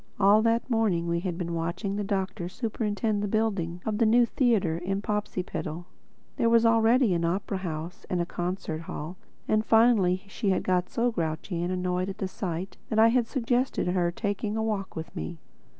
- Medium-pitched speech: No, high, 195 Hz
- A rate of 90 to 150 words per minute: No, average, 185 wpm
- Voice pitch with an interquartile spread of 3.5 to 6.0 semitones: Yes, average, 4.1 semitones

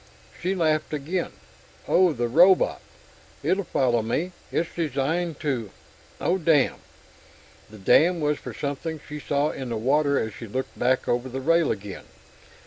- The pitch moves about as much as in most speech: Yes, average, 4.6 semitones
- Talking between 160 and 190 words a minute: No, average, 150 wpm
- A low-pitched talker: No, medium, 145 Hz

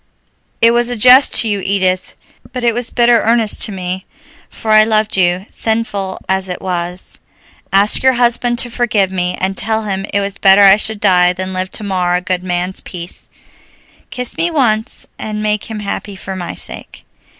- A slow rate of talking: No, average, 190 wpm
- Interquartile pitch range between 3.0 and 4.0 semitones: Yes, average, 3.4 semitones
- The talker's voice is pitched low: No, high, 200 Hz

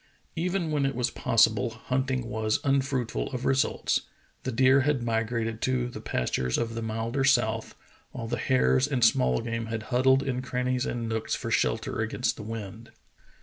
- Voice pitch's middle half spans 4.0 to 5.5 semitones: No, average, 2.7 semitones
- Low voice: Yes, low, 120 Hz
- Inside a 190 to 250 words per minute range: No, average, 170 wpm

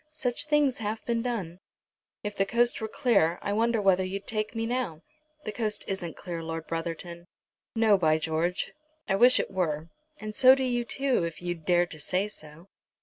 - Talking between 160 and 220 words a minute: Yes, average, 190 wpm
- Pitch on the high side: Yes, high, 195 Hz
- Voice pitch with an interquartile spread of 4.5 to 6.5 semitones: Yes, wide, 5.4 semitones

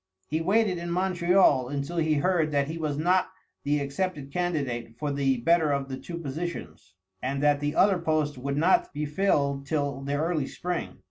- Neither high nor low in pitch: Yes, medium, 150 Hz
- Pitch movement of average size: Yes, average, 3.7 semitones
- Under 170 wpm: No, average, 185 wpm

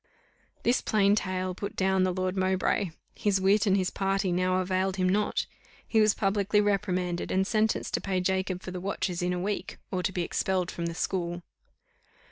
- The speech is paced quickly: No, average, 190 wpm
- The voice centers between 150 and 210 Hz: Yes, high, 190 Hz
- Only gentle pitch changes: Yes, narrow, 1.4 semitones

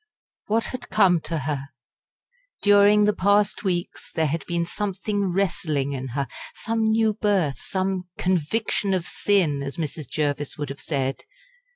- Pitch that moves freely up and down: Yes, wide, 5.7 semitones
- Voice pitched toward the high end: No, medium, 180 Hz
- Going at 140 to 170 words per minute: Yes, average, 150 wpm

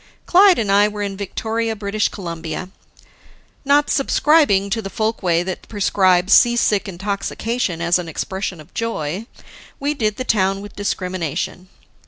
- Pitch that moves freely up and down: No, average, 3.6 semitones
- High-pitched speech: Yes, high, 200 Hz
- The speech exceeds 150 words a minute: No, average, 140 wpm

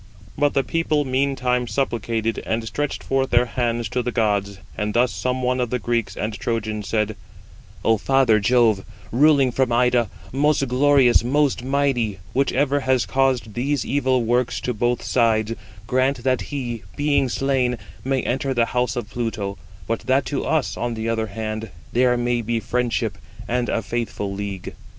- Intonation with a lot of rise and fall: No, average, 2.8 semitones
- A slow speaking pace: No, average, 165 wpm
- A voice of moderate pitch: No, low, 120 Hz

